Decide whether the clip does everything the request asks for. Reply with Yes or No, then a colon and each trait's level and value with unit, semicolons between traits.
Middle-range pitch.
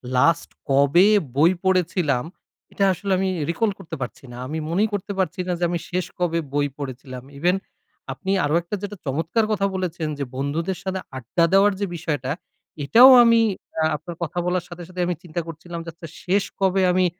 Yes: medium, 175 Hz